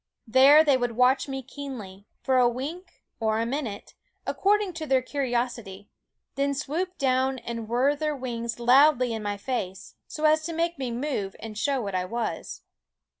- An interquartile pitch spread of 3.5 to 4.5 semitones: Yes, average, 3.8 semitones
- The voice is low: No, very high, 255 Hz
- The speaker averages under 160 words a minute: No, average, 175 wpm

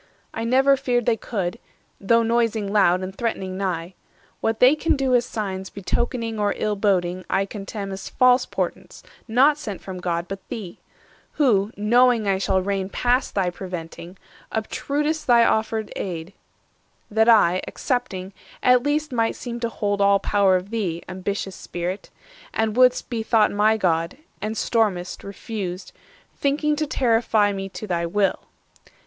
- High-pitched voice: Yes, high, 210 Hz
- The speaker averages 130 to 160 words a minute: Yes, average, 155 wpm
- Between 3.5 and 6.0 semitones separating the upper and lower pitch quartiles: Yes, average, 3.9 semitones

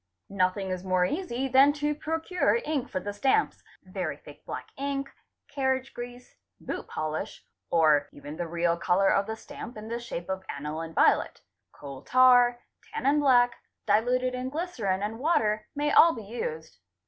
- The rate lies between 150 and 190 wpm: Yes, average, 160 wpm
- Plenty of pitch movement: Yes, wide, 6.5 semitones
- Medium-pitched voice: No, high, 225 Hz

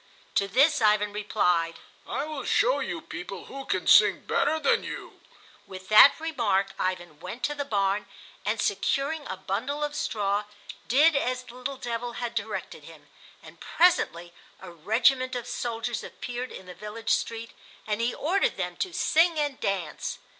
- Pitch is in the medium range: No, high, 230 Hz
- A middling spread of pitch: No, wide, 5.8 semitones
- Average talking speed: Yes, average, 165 wpm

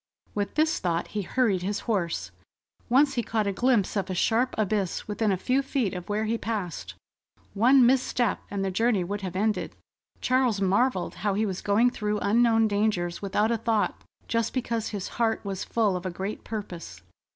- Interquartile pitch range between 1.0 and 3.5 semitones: Yes, average, 3.2 semitones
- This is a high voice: Yes, high, 210 Hz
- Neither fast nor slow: Yes, average, 185 wpm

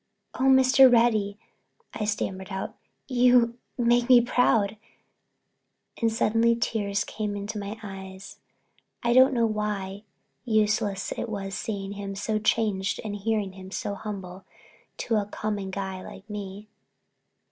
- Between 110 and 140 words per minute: Yes, slow, 135 wpm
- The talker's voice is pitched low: No, high, 210 Hz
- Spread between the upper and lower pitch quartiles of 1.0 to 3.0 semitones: Yes, average, 2.7 semitones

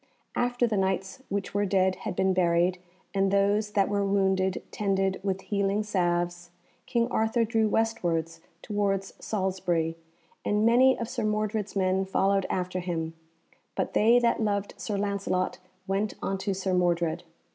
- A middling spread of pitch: No, narrow, 2.2 semitones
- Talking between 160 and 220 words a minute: No, average, 145 wpm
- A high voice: Yes, high, 195 Hz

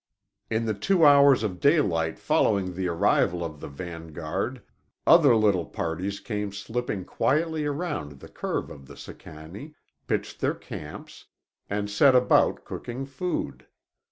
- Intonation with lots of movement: Yes, wide, 8.4 semitones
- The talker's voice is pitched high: No, low, 105 Hz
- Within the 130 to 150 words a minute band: Yes, slow, 135 wpm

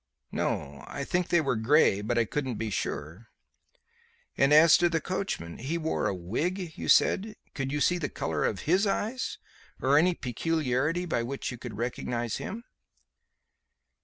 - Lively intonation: Yes, wide, 6.8 semitones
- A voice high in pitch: No, medium, 140 Hz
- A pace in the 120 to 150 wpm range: No, average, 165 wpm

